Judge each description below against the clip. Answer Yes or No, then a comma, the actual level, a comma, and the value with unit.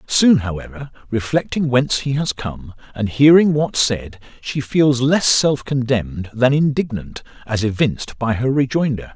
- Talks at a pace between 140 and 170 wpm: Yes, average, 150 wpm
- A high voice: No, low, 130 Hz